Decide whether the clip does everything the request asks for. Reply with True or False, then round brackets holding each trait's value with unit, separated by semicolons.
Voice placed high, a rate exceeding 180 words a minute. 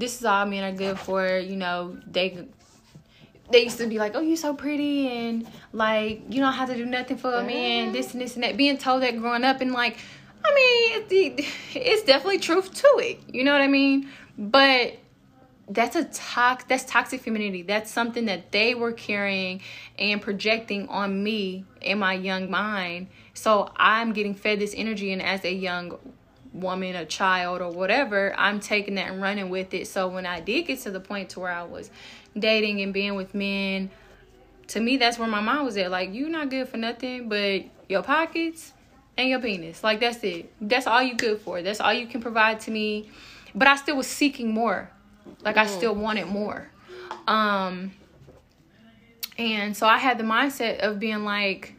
True (220 Hz; 200 wpm)